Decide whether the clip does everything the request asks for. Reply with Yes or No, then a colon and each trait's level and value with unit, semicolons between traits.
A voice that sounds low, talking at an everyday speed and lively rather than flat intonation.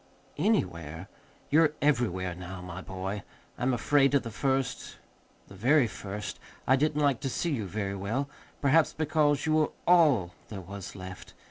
Yes: low, 120 Hz; average, 155 wpm; wide, 7.3 semitones